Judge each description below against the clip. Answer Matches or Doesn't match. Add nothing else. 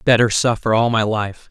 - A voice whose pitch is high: Doesn't match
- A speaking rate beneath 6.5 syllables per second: Matches